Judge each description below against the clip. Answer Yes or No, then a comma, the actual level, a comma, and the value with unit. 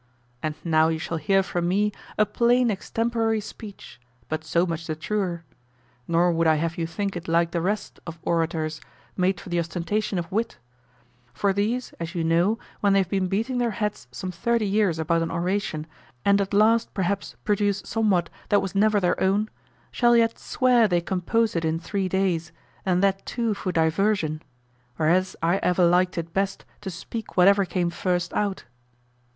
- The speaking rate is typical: Yes, average, 180 wpm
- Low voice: No, high, 190 Hz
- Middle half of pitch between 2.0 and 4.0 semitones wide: Yes, average, 3.7 semitones